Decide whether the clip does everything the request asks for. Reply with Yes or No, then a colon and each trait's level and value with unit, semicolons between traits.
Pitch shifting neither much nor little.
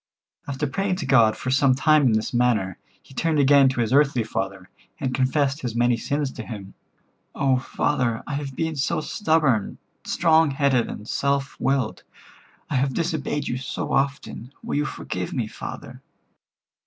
Yes: average, 3.1 semitones